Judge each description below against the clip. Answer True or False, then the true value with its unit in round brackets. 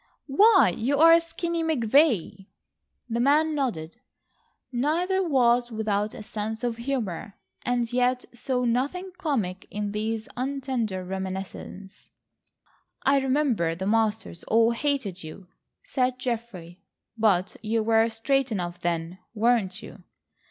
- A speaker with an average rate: False (120 wpm)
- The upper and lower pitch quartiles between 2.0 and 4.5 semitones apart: False (5.2 semitones)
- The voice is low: False (230 Hz)